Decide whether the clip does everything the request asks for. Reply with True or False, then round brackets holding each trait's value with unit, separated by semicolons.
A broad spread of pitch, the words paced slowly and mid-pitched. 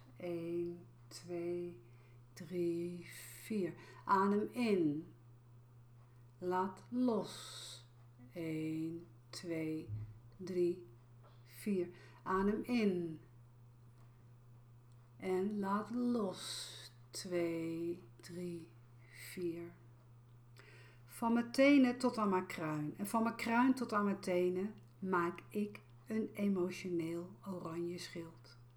True (7.6 semitones; 85 wpm; 170 Hz)